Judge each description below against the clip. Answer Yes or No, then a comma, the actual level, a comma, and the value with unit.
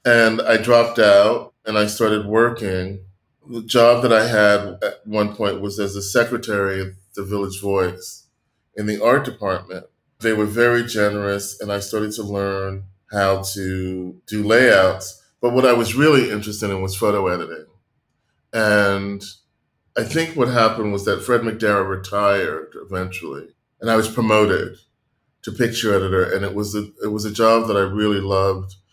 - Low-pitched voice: Yes, low, 105 Hz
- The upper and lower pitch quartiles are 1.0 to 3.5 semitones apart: Yes, narrow, 2.4 semitones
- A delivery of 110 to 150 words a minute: No, average, 170 wpm